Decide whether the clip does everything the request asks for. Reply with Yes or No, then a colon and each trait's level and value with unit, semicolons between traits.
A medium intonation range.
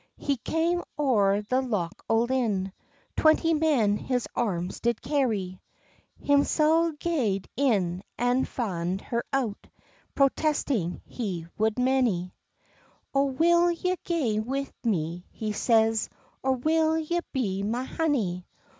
No: wide, 6.1 semitones